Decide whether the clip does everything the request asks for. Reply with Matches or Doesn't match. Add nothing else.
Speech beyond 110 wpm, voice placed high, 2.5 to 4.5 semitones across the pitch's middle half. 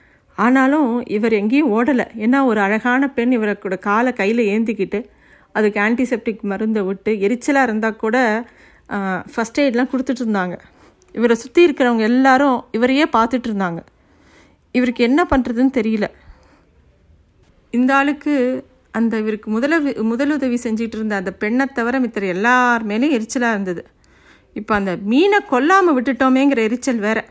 Matches